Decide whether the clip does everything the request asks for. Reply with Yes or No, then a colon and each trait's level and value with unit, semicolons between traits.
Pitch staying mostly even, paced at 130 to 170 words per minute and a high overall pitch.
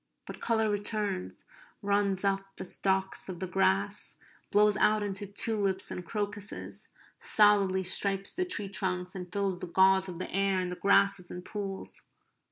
Yes: narrow, 1.8 semitones; average, 160 wpm; high, 195 Hz